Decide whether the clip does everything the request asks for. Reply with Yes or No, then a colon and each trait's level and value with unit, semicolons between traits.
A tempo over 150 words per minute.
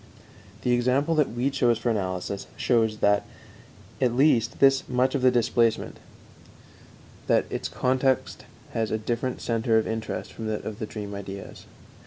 No: average, 145 wpm